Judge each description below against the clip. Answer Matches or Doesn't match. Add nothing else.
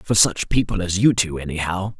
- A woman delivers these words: Doesn't match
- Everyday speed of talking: Doesn't match